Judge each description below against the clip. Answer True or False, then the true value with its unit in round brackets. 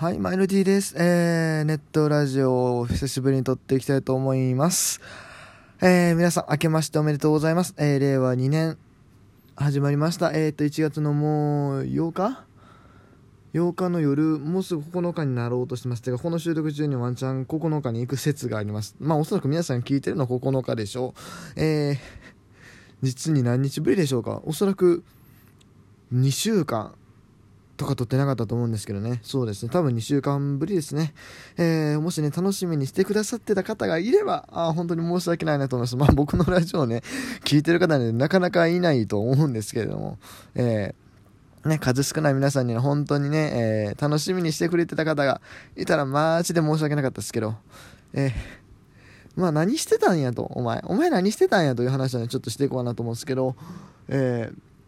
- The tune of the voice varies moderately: True (4.9 semitones)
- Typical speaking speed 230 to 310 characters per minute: False (390 characters per minute)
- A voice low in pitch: False (145 Hz)